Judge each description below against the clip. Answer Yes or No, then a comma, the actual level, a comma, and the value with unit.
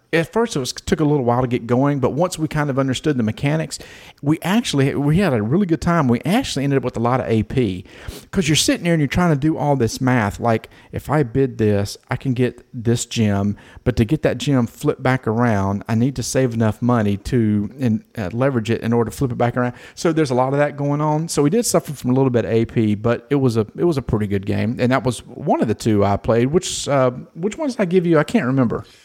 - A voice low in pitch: Yes, low, 130 Hz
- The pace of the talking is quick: Yes, fast, 270 wpm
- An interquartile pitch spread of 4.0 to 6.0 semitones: Yes, average, 4.6 semitones